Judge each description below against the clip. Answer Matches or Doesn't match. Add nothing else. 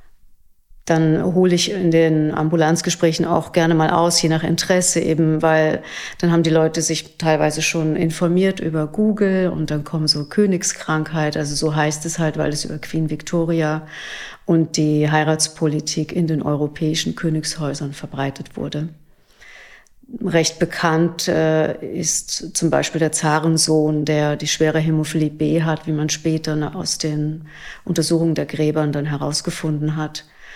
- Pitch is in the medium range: Matches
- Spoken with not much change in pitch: Matches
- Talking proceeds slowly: Doesn't match